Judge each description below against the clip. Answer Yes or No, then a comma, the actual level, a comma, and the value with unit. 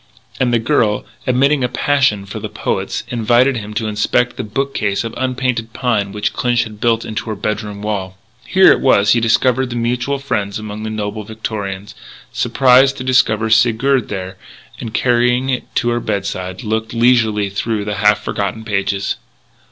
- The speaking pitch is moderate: No, low, 110 Hz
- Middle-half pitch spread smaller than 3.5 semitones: Yes, average, 3.1 semitones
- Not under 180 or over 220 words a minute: No, average, 165 wpm